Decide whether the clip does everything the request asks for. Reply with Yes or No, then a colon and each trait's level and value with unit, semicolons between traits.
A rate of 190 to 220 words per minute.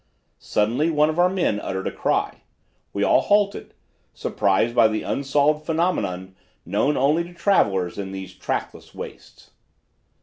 No: average, 140 wpm